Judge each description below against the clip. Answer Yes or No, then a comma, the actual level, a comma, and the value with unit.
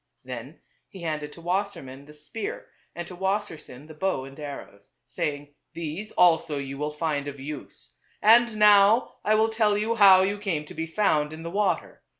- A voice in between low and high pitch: Yes, medium, 165 Hz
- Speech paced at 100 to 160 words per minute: No, average, 185 wpm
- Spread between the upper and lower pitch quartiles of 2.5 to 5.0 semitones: No, wide, 5.6 semitones